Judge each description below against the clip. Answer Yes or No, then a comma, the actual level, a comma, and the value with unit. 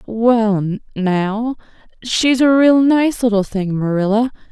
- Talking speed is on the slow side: Yes, slow, 120 wpm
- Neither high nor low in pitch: No, high, 225 Hz